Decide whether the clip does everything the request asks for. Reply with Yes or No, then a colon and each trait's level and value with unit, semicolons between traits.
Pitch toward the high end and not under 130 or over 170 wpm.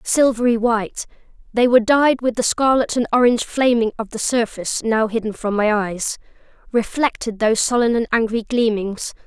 Yes: high, 230 Hz; average, 160 wpm